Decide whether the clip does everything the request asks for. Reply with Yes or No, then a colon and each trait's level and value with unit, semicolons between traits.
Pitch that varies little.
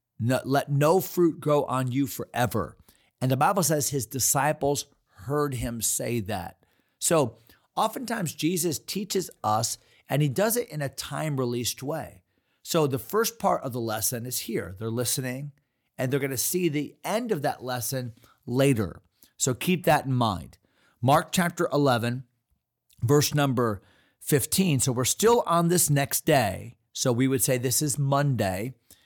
No: average, 4.0 semitones